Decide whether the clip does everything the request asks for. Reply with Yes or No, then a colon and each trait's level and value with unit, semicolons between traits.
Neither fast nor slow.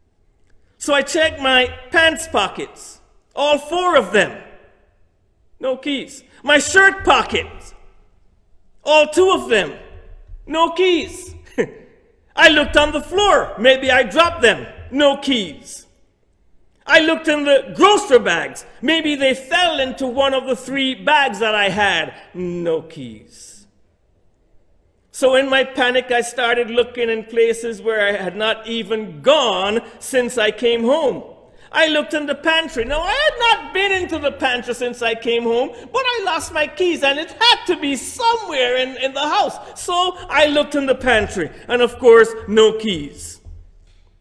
Yes: average, 155 wpm